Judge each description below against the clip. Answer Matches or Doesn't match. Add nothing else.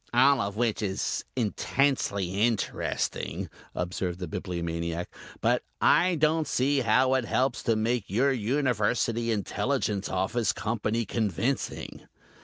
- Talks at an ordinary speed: Doesn't match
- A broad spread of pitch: Doesn't match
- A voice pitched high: Doesn't match